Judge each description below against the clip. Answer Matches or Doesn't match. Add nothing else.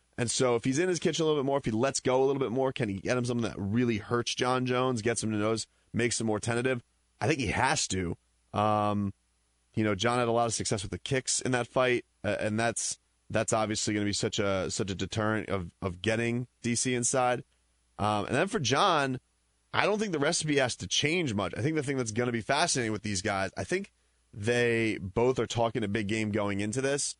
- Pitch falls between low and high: Doesn't match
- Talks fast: Matches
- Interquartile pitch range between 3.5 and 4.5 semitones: Matches